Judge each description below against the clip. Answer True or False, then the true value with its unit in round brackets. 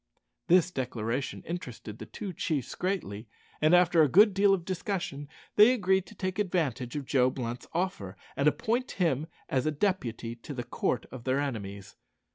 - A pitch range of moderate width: False (7.0 semitones)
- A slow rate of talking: False (170 wpm)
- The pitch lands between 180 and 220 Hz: False (150 Hz)